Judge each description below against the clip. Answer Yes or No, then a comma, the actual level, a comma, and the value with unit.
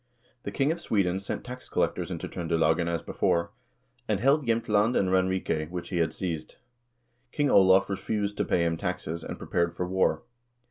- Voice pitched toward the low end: Yes, very low, 95 Hz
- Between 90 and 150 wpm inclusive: No, average, 175 wpm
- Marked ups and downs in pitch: No, average, 3.7 semitones